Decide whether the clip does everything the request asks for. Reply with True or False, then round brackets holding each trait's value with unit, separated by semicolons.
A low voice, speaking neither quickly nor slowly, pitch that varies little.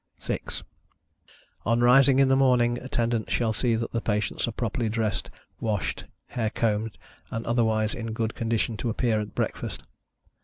True (115 Hz; 155 wpm; 1.6 semitones)